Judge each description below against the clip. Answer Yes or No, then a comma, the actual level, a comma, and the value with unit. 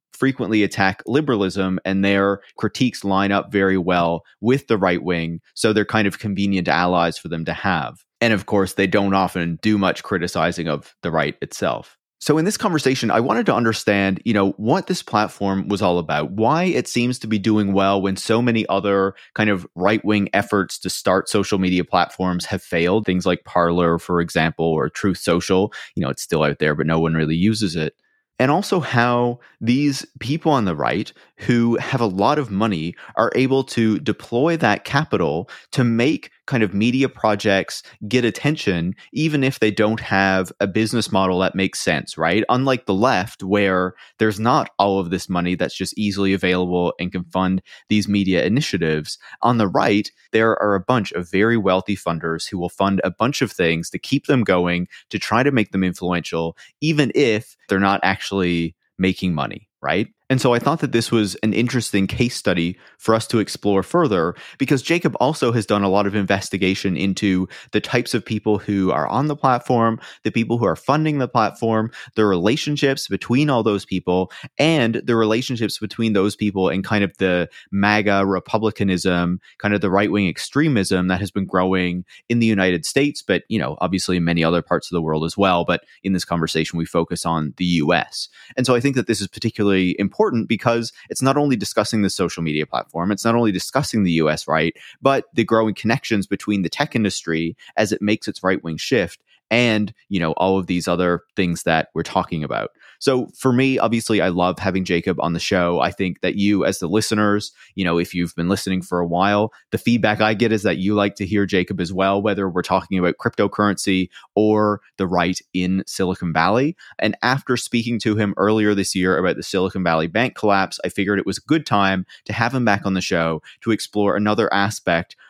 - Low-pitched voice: Yes, low, 100 Hz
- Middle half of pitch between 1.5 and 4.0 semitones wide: Yes, average, 3.7 semitones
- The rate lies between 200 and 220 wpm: Yes, fast, 205 wpm